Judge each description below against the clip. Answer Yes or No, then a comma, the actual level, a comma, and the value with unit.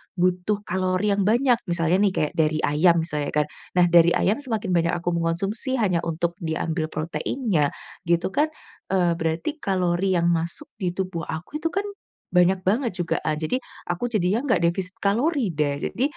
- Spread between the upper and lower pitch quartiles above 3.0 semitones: Yes, average, 3.7 semitones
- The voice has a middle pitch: Yes, medium, 180 Hz